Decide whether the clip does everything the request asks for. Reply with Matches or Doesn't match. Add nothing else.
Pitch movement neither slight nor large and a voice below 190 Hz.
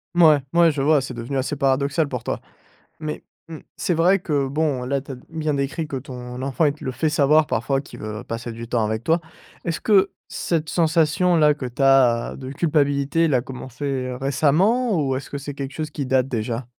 Matches